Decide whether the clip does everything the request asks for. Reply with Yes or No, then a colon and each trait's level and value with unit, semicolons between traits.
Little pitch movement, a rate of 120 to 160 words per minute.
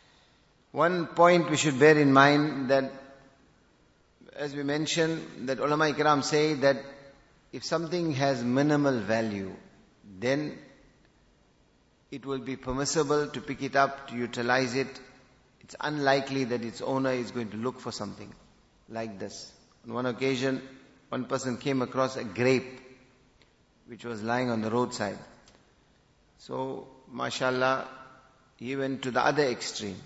Yes: narrow, 2.1 semitones; average, 140 wpm